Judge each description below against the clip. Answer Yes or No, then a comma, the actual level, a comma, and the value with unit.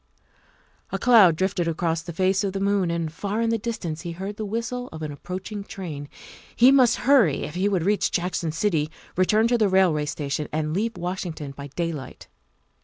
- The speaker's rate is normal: Yes, average, 190 wpm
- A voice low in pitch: No, medium, 185 Hz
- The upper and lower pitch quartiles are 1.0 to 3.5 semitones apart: No, average, 4.5 semitones